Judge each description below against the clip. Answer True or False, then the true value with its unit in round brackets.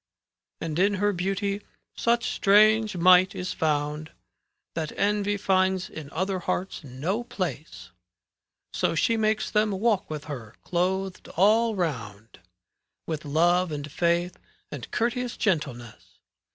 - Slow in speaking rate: True (125 wpm)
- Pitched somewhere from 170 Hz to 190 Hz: True (185 Hz)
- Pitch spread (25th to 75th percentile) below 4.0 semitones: False (4.7 semitones)